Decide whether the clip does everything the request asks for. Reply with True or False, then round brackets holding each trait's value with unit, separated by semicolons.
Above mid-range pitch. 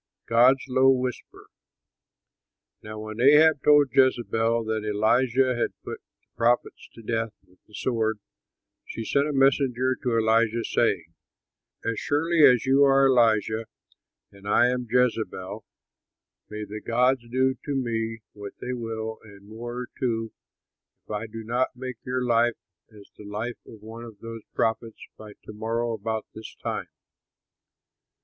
False (115 Hz)